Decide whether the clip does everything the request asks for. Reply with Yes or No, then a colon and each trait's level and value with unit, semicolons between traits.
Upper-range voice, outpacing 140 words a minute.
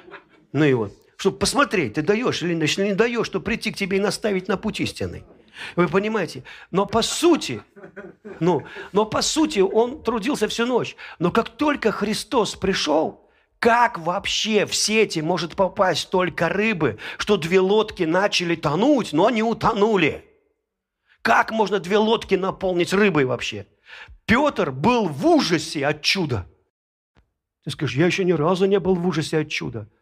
Yes: high, 200 Hz; average, 155 wpm